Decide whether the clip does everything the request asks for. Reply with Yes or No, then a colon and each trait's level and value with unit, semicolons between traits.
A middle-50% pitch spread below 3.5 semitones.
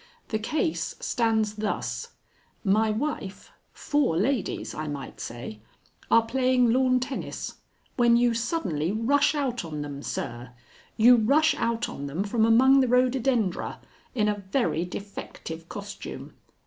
No: average, 5.1 semitones